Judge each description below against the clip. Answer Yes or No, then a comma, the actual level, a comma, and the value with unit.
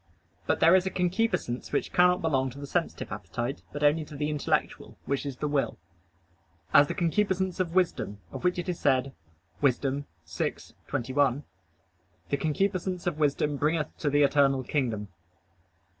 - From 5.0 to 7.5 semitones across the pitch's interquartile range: No, average, 4.5 semitones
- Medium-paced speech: Yes, average, 160 wpm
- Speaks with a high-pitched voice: No, medium, 145 Hz